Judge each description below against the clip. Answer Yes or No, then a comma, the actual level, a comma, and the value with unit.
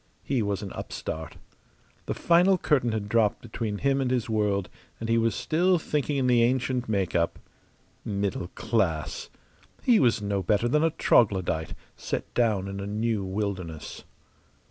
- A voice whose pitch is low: Yes, low, 110 Hz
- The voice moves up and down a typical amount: Yes, average, 4.4 semitones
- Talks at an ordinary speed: Yes, average, 160 wpm